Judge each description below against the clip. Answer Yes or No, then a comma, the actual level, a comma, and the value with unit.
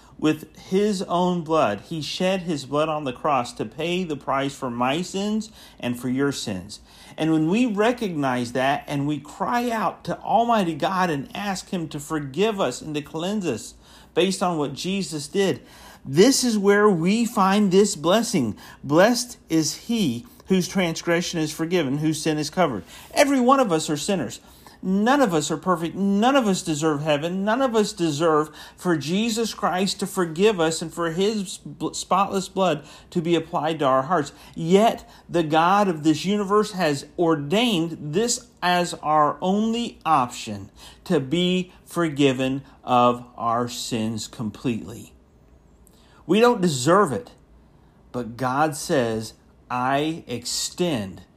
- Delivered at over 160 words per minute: No, average, 155 wpm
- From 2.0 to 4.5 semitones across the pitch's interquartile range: No, average, 5.1 semitones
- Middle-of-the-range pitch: Yes, medium, 165 Hz